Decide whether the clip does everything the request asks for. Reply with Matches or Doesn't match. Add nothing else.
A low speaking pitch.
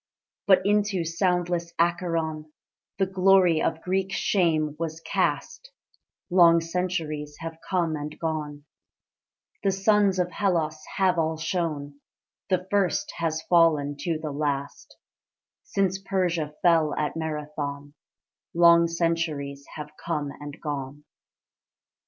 Doesn't match